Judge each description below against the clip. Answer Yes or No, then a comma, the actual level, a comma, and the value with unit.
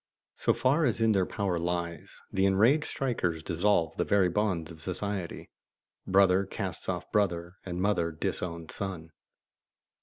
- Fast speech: No, average, 145 wpm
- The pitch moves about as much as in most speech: Yes, average, 3.3 semitones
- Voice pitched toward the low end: Yes, very low, 95 Hz